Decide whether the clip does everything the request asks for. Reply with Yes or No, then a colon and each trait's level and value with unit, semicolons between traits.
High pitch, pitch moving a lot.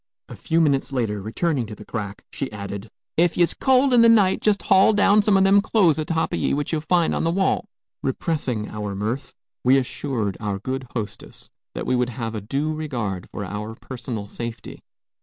No: low, 135 Hz; wide, 7.9 semitones